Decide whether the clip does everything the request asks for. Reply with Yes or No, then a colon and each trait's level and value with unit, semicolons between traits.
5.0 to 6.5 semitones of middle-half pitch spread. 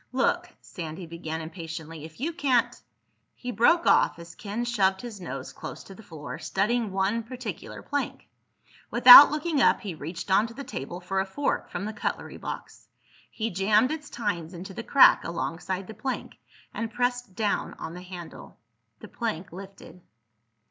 Yes: wide, 5.5 semitones